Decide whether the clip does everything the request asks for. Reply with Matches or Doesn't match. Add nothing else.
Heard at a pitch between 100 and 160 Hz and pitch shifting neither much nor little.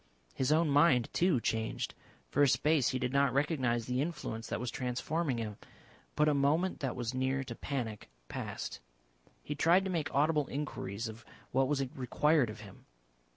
Matches